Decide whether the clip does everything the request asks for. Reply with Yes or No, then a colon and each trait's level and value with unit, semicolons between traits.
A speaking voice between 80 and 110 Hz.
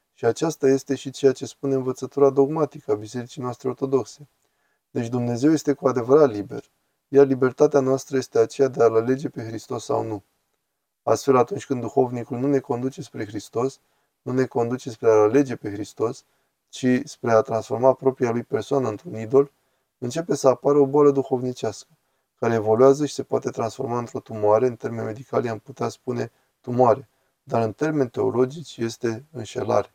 No: low, 130 Hz